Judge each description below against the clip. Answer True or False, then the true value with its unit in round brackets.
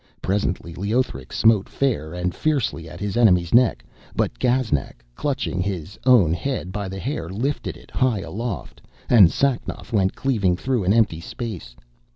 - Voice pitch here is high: False (100 Hz)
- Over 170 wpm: False (155 wpm)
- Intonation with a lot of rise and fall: True (5.7 semitones)